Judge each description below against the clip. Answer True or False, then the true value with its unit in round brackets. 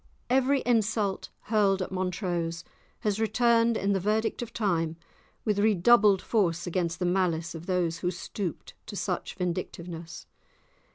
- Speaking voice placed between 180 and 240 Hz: True (190 Hz)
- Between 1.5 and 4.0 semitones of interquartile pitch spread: True (3.7 semitones)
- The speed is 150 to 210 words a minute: False (135 wpm)